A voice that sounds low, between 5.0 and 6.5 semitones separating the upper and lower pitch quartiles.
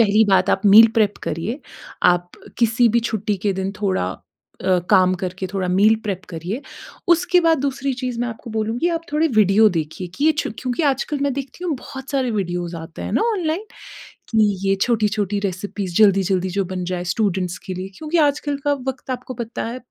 No: high, 215 Hz; wide, 5.5 semitones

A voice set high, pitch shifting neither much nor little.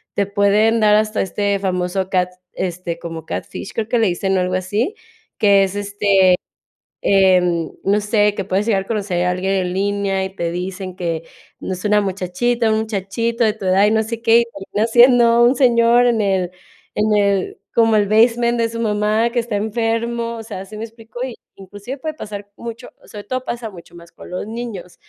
Yes: high, 205 Hz; average, 3.2 semitones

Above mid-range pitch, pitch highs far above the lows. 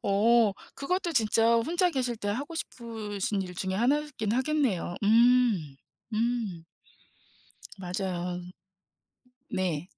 No: high, 225 Hz; average, 4.8 semitones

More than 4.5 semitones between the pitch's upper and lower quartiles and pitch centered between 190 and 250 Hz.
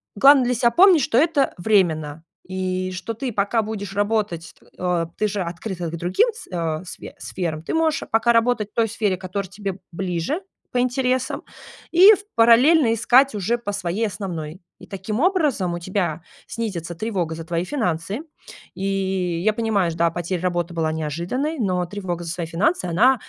Yes: average, 5.1 semitones; high, 195 Hz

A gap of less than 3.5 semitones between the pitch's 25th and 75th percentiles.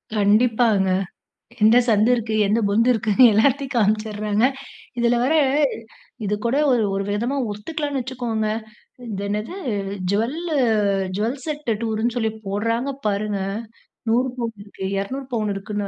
Yes: average, 2.9 semitones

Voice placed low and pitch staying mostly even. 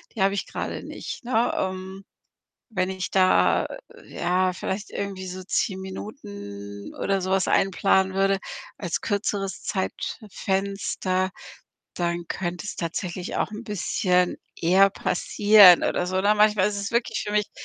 No: high, 190 Hz; narrow, 1.7 semitones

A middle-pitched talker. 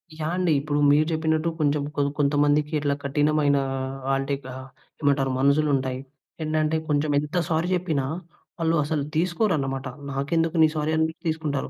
Yes: medium, 150 Hz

